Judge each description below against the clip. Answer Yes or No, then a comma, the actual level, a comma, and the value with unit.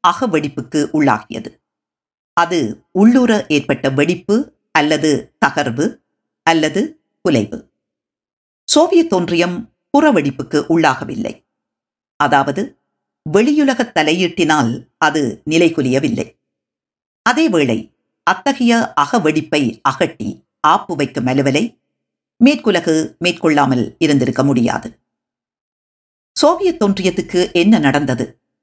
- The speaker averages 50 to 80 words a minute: Yes, slow, 75 wpm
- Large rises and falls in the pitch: Yes, wide, 7.2 semitones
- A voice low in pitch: No, medium, 160 Hz